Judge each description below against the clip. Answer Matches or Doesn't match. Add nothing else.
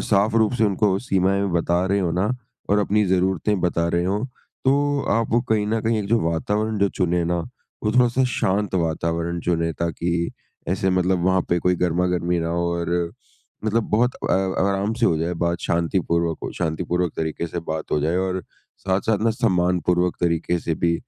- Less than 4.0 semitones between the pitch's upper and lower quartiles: Matches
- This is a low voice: Matches